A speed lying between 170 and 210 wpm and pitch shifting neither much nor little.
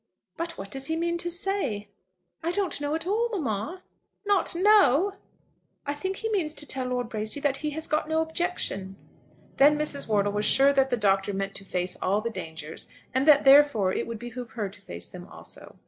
No: fast, 205 wpm; wide, 8.0 semitones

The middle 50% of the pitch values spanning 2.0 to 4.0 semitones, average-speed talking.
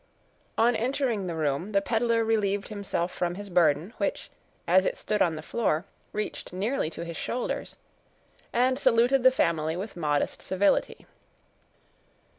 No: wide, 5.5 semitones; average, 145 wpm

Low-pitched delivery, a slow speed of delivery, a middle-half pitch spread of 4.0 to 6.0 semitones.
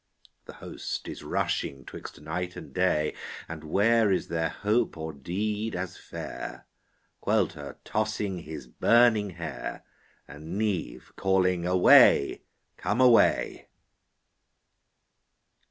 Yes: very low, 90 Hz; slow, 105 wpm; average, 4.8 semitones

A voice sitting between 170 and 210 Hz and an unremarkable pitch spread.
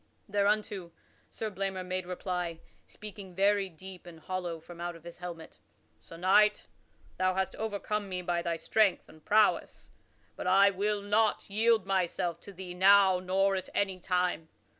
No: high, 190 Hz; narrow, 2.3 semitones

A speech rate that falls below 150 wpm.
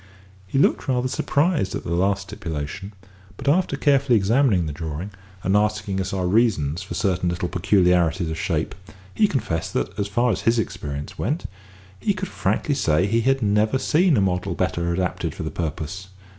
No: average, 180 wpm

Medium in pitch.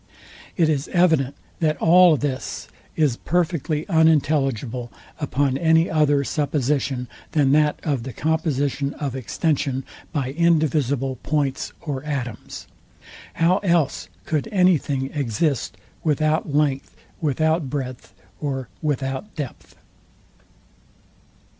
Yes: medium, 145 Hz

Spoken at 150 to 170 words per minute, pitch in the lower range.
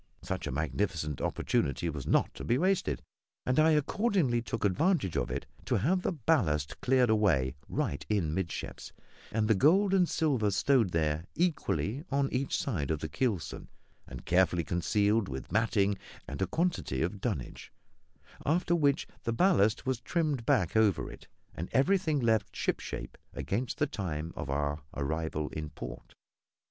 Yes: average, 155 wpm; low, 105 Hz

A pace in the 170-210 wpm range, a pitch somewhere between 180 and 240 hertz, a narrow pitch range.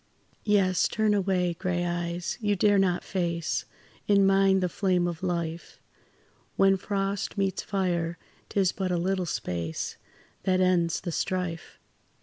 No: slow, 135 wpm; medium, 185 Hz; narrow, 2.1 semitones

